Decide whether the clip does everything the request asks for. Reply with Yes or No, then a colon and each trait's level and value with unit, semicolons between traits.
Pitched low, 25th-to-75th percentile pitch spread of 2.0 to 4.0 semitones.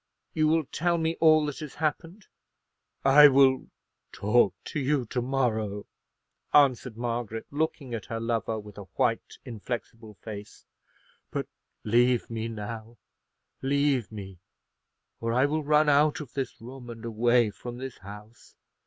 No: low, 120 Hz; average, 4.4 semitones